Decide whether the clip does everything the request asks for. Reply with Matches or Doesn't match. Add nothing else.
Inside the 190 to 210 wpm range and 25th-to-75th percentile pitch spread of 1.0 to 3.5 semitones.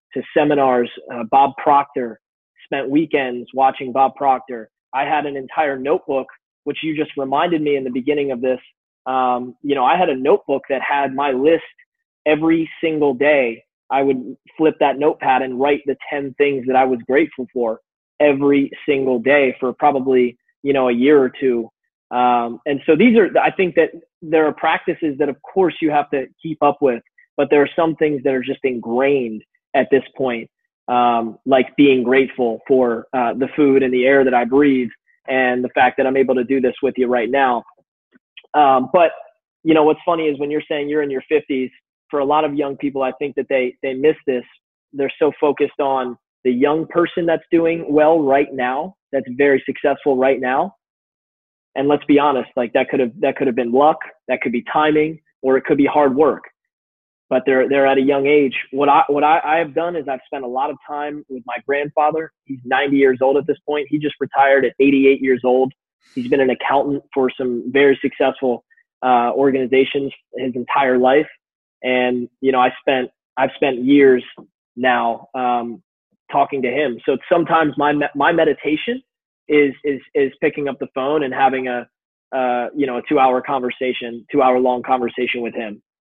Matches